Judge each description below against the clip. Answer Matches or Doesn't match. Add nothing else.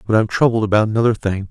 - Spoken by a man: Matches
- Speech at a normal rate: Doesn't match